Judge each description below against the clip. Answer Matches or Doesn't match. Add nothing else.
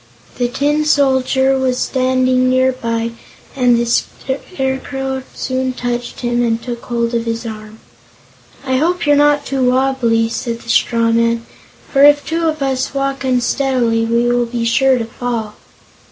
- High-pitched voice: Matches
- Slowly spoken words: Doesn't match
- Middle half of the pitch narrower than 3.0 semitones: Matches